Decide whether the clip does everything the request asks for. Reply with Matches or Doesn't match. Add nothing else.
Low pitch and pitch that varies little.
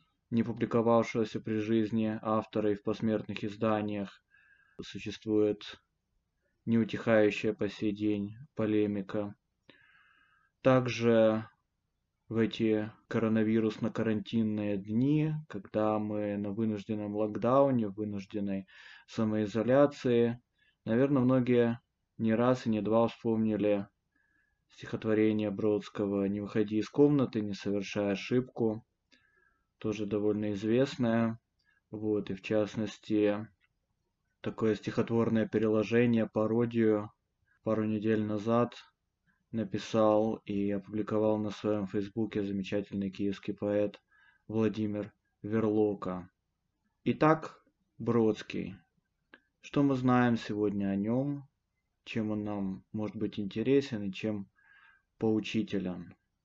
Matches